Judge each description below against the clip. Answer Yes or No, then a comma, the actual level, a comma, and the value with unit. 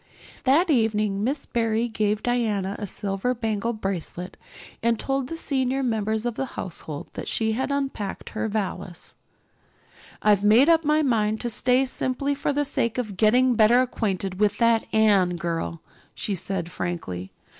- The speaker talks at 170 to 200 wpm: No, average, 155 wpm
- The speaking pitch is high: Yes, high, 220 Hz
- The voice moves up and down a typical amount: Yes, average, 4.2 semitones